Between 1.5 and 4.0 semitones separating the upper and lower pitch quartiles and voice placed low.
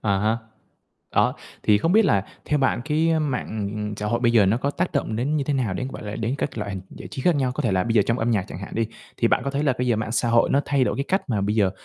No: average, 4.9 semitones; low, 120 Hz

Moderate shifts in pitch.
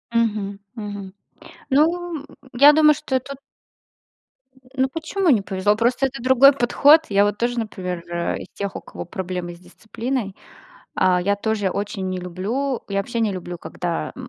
No: wide, 5.7 semitones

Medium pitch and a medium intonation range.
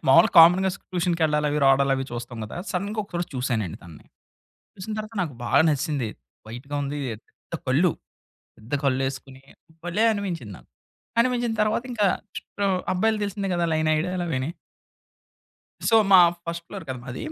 No: medium, 165 Hz; wide, 6.3 semitones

